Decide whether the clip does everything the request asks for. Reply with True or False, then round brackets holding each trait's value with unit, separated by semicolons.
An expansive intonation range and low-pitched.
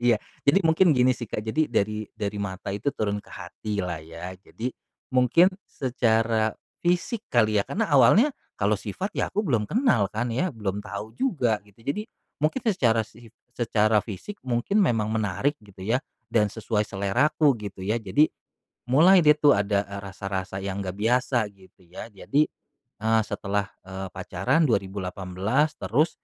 True (5.7 semitones; 110 Hz)